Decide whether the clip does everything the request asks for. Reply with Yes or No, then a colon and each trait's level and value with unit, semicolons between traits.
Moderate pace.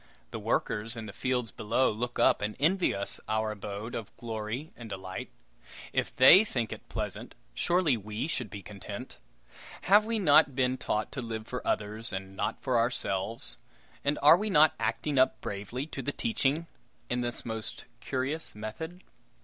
Yes: average, 170 wpm